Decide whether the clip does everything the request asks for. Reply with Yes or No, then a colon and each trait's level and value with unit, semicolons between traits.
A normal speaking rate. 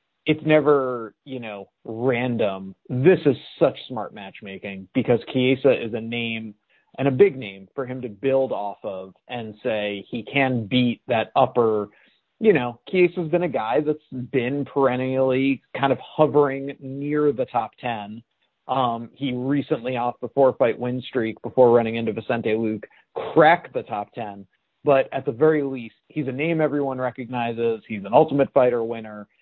Yes: average, 165 wpm